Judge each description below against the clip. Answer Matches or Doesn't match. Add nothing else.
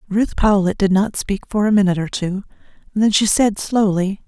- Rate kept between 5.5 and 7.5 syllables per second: Doesn't match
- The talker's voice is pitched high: Matches